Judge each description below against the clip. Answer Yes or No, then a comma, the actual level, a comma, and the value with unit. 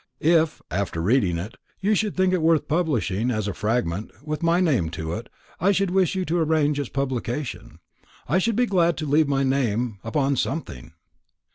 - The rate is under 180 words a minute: No, average, 185 wpm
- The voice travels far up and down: Yes, wide, 7.3 semitones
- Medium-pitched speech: Yes, medium, 145 Hz